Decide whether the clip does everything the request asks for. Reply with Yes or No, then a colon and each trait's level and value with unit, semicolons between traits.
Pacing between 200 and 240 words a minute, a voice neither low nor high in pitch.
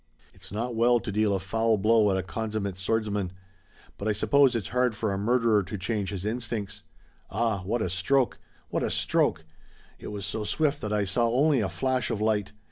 No: fast, 205 wpm; low, 110 Hz